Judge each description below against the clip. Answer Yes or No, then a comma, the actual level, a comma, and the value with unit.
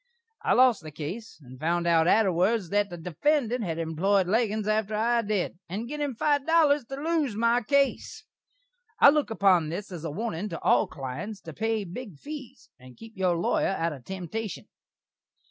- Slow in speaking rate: No, average, 180 wpm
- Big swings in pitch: Yes, wide, 5.7 semitones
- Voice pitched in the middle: No, high, 205 Hz